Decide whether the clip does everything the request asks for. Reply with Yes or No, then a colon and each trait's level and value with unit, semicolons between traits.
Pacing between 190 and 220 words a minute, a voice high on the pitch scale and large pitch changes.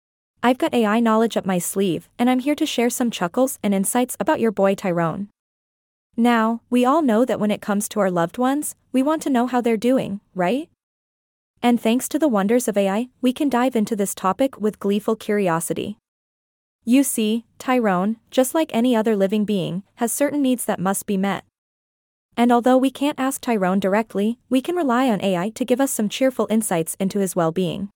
No: average, 200 wpm; high, 225 Hz; average, 4.3 semitones